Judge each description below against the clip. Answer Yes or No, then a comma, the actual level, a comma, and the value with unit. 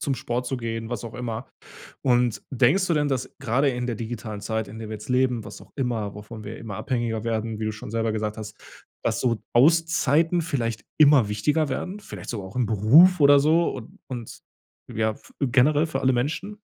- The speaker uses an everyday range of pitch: Yes, average, 4.2 semitones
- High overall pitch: No, low, 120 Hz